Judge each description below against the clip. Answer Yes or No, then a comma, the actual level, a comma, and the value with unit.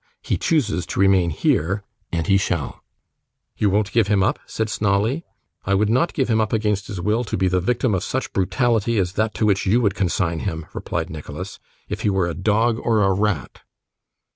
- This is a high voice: No, low, 100 Hz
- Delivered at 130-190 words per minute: No, fast, 205 wpm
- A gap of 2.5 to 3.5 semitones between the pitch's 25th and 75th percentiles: Yes, average, 3.1 semitones